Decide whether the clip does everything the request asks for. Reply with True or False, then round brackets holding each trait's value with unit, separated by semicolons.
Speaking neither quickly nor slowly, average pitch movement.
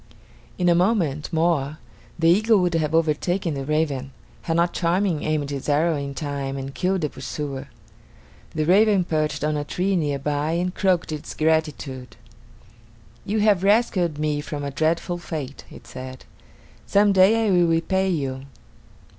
True (160 wpm; 3.7 semitones)